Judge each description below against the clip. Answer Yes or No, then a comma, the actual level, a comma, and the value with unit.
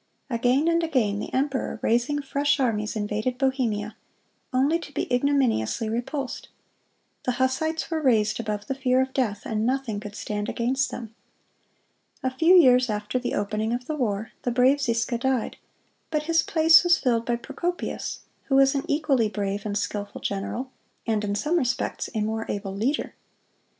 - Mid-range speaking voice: No, very high, 250 Hz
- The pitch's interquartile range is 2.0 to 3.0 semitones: No, average, 4.4 semitones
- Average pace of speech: Yes, average, 165 wpm